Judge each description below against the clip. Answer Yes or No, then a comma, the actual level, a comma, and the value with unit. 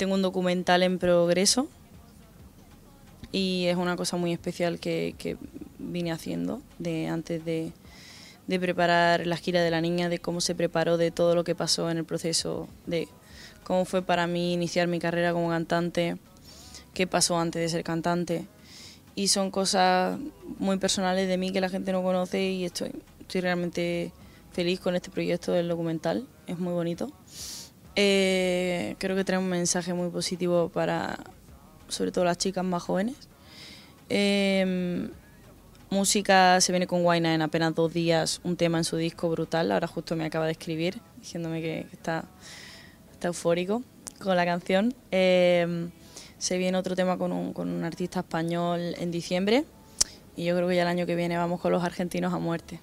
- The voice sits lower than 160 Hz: No, medium, 175 Hz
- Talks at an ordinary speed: Yes, average, 175 wpm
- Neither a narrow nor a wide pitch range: No, narrow, 1.6 semitones